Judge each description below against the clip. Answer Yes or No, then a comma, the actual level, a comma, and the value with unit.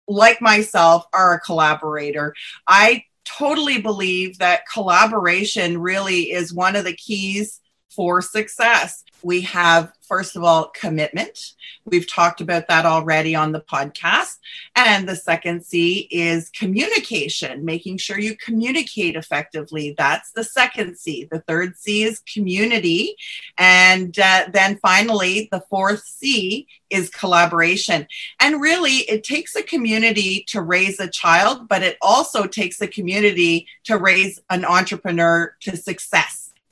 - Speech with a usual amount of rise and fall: Yes, average, 4.0 semitones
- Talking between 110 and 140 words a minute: Yes, slow, 135 wpm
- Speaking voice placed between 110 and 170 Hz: No, high, 190 Hz